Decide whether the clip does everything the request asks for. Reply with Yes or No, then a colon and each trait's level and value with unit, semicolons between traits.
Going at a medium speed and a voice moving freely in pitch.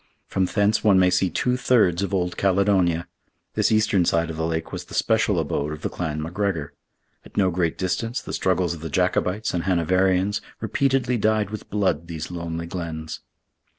No: average, 185 wpm; average, 3.5 semitones